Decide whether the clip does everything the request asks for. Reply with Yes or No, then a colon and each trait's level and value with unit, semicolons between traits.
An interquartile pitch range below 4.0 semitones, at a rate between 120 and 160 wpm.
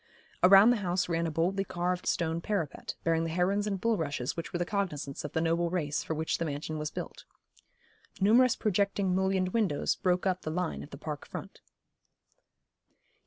No: average, 3.3 semitones; average, 180 wpm